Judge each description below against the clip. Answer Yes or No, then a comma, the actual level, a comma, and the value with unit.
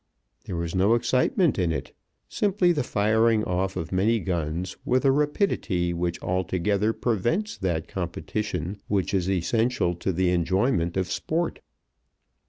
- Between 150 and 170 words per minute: No, average, 140 wpm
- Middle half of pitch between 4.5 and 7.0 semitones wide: Yes, average, 5.1 semitones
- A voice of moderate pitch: No, very low, 95 Hz